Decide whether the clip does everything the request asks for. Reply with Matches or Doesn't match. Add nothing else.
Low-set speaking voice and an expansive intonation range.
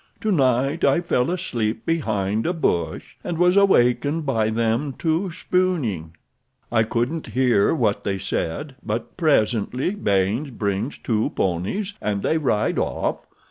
Matches